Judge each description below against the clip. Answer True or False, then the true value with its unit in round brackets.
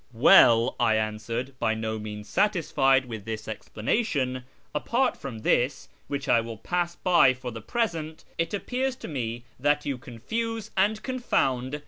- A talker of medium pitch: False (130 Hz)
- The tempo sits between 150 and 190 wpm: True (165 wpm)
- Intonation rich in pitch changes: True (7.4 semitones)